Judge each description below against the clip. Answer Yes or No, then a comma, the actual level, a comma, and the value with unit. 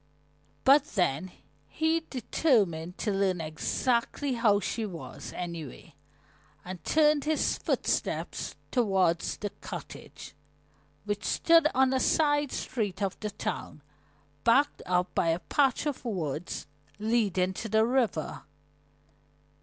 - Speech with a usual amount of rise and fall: No, wide, 6.5 semitones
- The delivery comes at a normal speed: No, slow, 115 wpm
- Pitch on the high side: Yes, high, 215 Hz